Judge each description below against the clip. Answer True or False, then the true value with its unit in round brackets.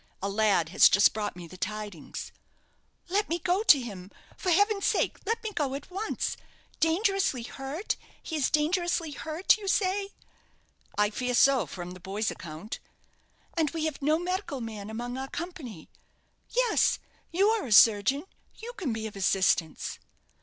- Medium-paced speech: True (160 wpm)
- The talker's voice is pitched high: True (275 Hz)